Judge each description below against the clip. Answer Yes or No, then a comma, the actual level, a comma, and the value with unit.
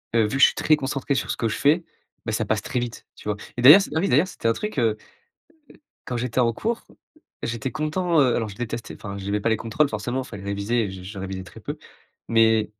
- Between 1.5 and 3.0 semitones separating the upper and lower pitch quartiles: No, average, 4.5 semitones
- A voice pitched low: Yes, low, 115 Hz